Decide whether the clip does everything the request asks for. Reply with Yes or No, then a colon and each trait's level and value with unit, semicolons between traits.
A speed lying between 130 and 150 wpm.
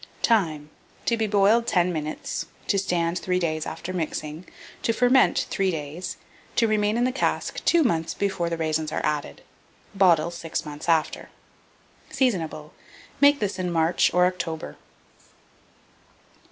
Yes: average, 140 wpm